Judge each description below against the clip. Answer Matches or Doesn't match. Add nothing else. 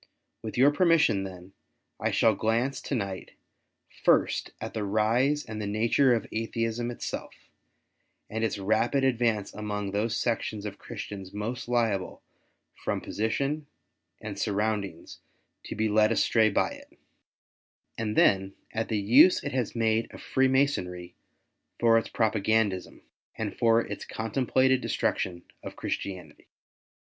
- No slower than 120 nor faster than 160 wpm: Matches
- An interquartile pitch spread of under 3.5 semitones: Matches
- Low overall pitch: Matches